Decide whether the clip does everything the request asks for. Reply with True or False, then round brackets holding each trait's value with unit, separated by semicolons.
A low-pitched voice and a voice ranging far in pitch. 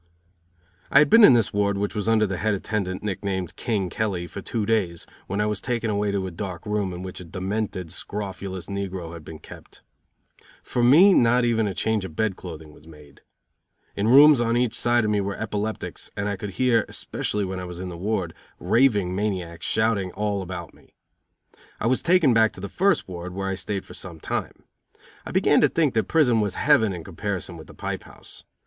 False (100 Hz; 3.4 semitones)